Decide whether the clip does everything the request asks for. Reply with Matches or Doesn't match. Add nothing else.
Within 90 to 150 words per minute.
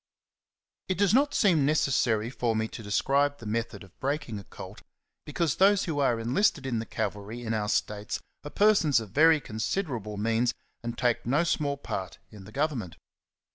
Doesn't match